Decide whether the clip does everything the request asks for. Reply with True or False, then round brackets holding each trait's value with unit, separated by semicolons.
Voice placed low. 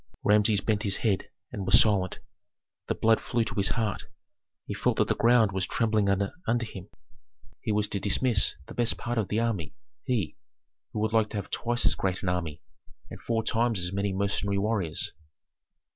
True (105 Hz)